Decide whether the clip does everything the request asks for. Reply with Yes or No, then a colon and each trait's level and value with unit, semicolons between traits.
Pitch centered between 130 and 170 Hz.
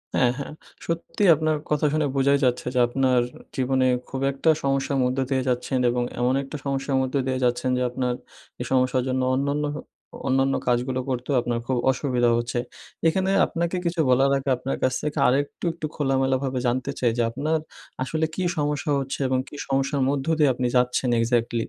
Yes: low, 135 Hz